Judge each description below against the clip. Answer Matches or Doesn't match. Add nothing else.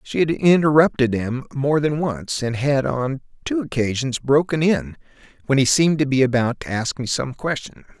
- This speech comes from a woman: Doesn't match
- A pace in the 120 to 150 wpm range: Doesn't match